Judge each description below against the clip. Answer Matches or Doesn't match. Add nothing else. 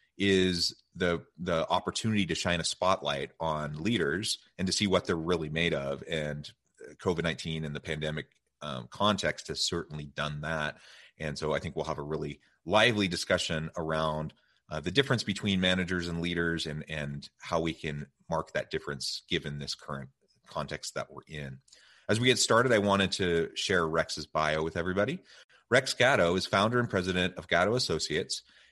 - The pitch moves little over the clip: Doesn't match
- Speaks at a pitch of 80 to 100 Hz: Matches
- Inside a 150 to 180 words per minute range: Matches